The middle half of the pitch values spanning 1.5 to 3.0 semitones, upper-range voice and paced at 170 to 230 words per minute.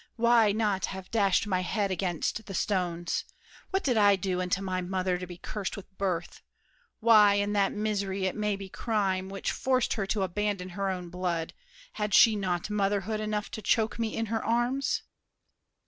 Yes: narrow, 2.4 semitones; high, 200 Hz; average, 180 wpm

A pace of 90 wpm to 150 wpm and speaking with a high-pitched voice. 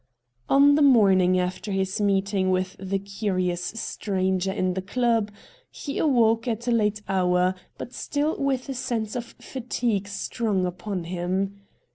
Yes: average, 145 wpm; high, 200 Hz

